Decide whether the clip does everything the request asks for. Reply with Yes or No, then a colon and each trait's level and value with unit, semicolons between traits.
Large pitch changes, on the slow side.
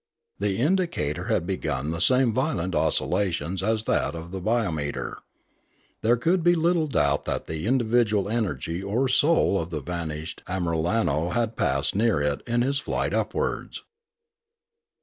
No: wide, 6.6 semitones; average, 145 wpm